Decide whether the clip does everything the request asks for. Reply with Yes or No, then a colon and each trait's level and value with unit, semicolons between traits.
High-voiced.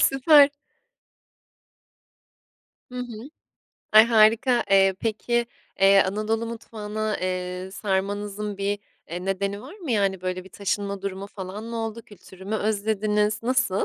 Yes: high, 210 Hz